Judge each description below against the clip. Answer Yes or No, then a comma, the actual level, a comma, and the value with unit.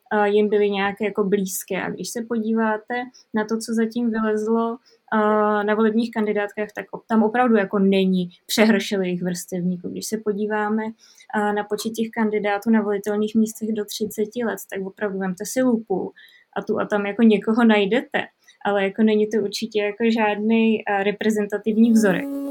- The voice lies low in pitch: No, high, 215 Hz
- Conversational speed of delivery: Yes, average, 155 wpm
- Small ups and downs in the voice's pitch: Yes, narrow, 1.5 semitones